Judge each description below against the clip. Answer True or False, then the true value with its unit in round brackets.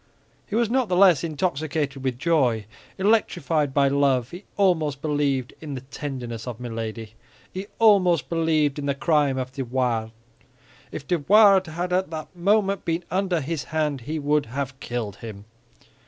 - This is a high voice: False (150 Hz)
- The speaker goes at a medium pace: True (165 wpm)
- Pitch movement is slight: False (5.2 semitones)